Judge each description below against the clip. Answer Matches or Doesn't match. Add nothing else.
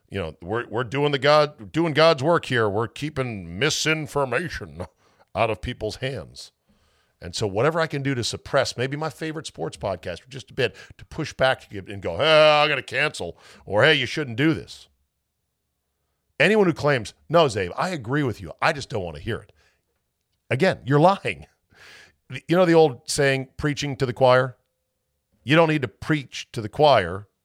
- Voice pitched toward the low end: Matches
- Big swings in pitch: Matches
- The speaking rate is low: Doesn't match